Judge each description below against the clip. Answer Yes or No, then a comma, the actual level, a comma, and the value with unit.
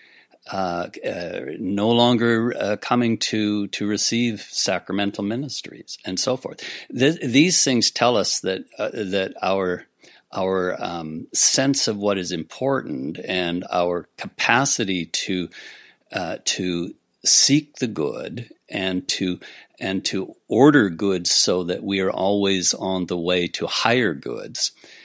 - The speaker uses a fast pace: No, slow, 135 wpm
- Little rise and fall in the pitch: No, average, 4.4 semitones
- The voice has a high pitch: No, low, 100 Hz